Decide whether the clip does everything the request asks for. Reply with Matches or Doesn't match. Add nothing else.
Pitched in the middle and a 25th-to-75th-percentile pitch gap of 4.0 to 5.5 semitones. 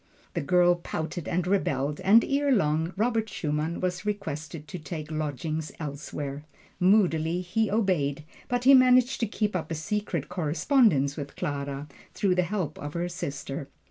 Matches